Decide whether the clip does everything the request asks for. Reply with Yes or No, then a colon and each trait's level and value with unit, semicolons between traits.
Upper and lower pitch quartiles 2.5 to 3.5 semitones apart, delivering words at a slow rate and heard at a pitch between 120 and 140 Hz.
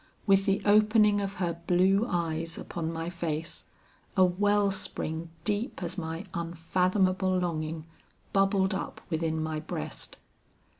No: average, 3.1 semitones; slow, 130 wpm; medium, 180 Hz